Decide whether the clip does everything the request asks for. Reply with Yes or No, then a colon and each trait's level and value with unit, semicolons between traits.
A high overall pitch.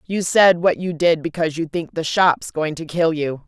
No: medium, 165 Hz